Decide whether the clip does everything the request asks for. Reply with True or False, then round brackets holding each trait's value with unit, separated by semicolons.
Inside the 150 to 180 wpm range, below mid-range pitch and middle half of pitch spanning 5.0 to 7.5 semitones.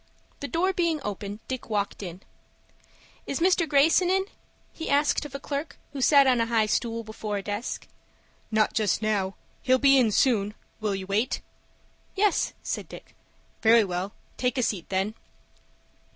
False (165 wpm; 230 Hz; 5.4 semitones)